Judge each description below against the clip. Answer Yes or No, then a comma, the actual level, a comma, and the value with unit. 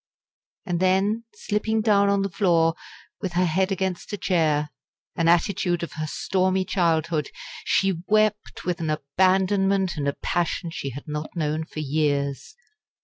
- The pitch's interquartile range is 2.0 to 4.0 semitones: Yes, average, 3.7 semitones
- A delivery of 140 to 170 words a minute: Yes, average, 150 wpm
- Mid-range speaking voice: Yes, medium, 175 Hz